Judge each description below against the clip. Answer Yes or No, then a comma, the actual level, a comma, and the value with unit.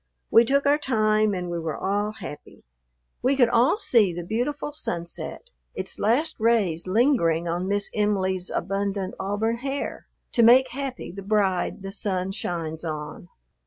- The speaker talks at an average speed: Yes, average, 155 wpm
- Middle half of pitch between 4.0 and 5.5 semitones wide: Yes, average, 4.7 semitones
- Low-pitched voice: No, high, 205 Hz